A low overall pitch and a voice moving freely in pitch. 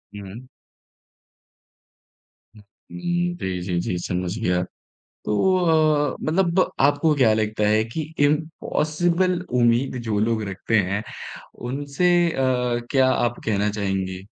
Yes: low, 120 Hz; wide, 6.7 semitones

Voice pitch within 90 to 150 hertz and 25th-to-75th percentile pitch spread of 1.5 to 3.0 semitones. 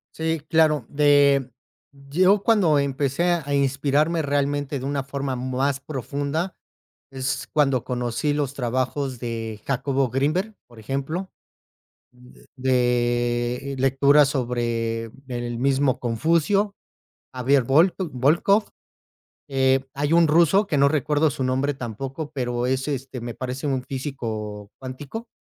Yes: low, 135 Hz; average, 2.7 semitones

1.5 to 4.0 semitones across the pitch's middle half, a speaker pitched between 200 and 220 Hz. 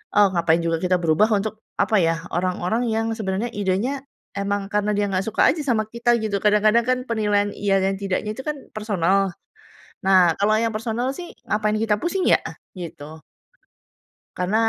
Yes: average, 2.8 semitones; high, 205 Hz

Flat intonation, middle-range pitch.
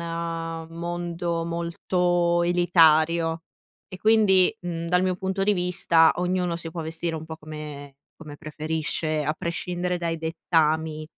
Yes: narrow, 1.7 semitones; medium, 170 Hz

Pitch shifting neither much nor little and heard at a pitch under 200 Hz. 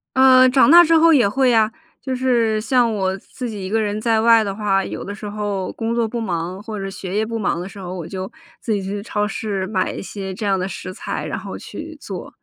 No: average, 3.2 semitones; high, 210 Hz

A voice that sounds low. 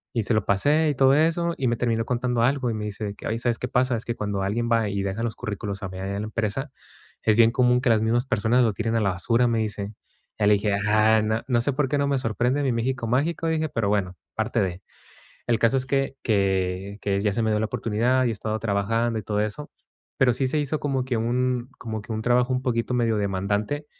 Yes: low, 115 Hz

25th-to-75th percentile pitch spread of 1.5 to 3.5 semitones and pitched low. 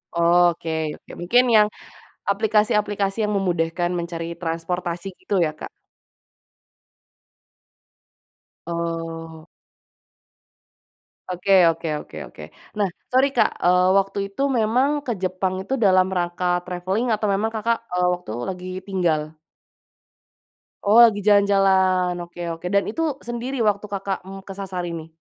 No: average, 3.1 semitones; medium, 185 Hz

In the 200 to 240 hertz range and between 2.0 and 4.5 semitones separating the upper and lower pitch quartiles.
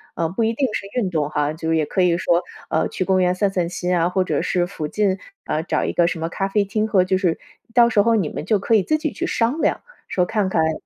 No: medium, 185 Hz; average, 3.8 semitones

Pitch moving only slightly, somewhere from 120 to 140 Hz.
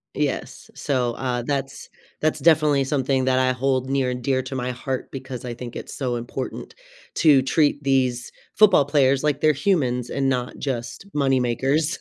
Yes: narrow, 2.1 semitones; low, 135 Hz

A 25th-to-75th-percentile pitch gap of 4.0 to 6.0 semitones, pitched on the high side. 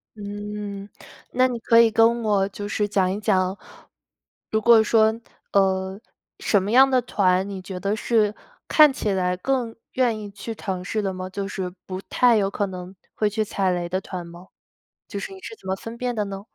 No: average, 3.0 semitones; high, 205 Hz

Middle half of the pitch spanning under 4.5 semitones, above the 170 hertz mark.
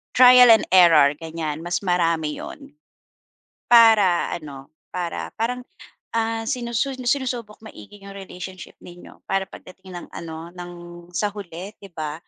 No: average, 5.2 semitones; high, 190 Hz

